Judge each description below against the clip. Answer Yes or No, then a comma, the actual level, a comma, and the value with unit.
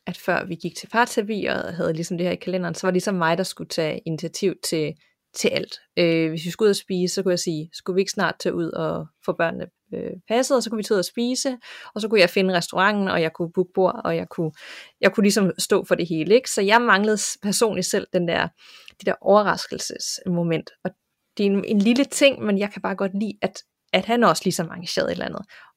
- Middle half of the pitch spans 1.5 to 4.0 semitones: Yes, average, 3.6 semitones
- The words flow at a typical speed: No, fast, 255 wpm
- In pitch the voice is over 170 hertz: Yes, medium, 185 Hz